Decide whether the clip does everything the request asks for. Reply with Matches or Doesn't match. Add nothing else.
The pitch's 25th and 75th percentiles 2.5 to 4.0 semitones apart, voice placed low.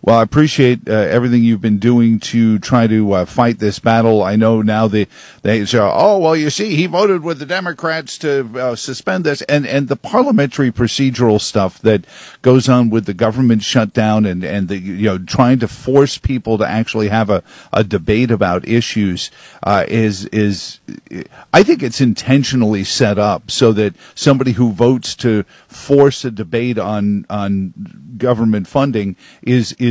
Matches